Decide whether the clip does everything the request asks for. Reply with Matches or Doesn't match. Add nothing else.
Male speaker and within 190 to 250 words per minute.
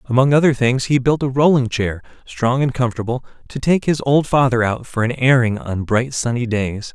Matches